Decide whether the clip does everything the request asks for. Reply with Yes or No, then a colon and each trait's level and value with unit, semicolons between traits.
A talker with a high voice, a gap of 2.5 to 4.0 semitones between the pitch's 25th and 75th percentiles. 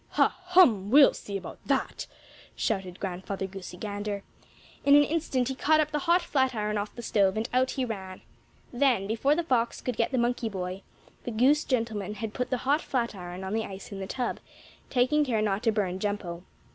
No: high, 225 Hz; average, 4.8 semitones